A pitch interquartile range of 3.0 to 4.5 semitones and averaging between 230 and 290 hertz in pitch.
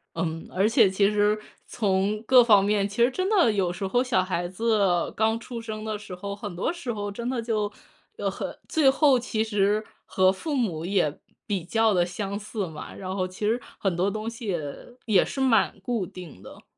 No: average, 3.3 semitones; high, 205 Hz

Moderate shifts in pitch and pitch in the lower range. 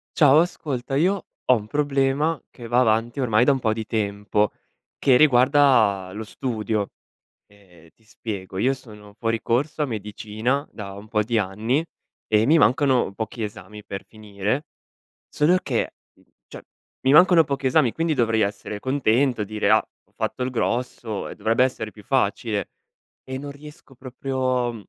Yes: average, 4.3 semitones; low, 120 Hz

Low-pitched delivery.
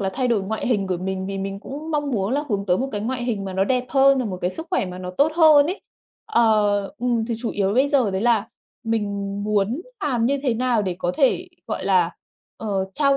No: high, 225 Hz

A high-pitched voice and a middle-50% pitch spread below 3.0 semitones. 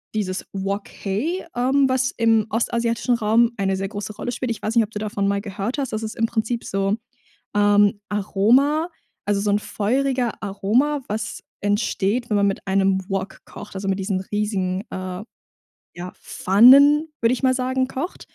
No: high, 215 Hz; average, 3.7 semitones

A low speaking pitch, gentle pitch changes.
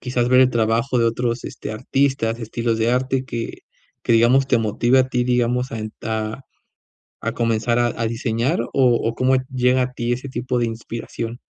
Yes: low, 120 Hz; narrow, 1.8 semitones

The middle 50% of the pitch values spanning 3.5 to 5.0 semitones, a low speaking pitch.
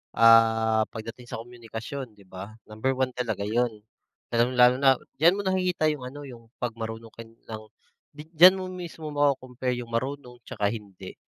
Yes: average, 4.0 semitones; low, 120 Hz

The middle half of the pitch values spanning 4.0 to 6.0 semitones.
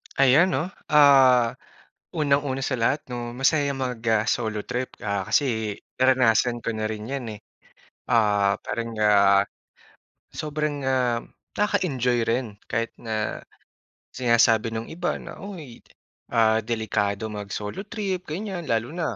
Yes: average, 4.5 semitones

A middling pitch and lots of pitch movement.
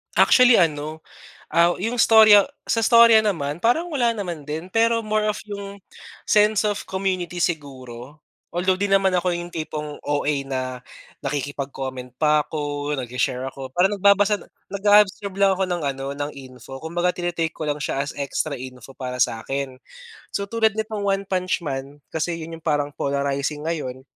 Yes: medium, 165 Hz; wide, 6.1 semitones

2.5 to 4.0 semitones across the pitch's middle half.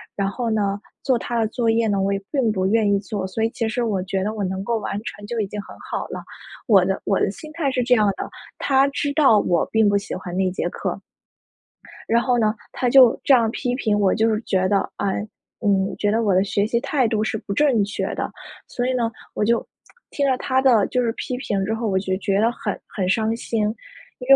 Yes: average, 3.5 semitones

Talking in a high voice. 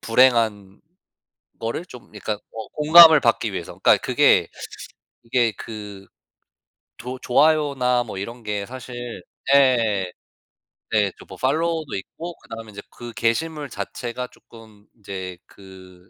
No: low, 115 Hz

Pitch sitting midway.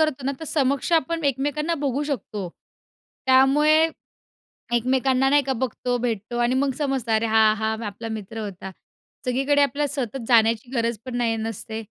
No: very high, 255 Hz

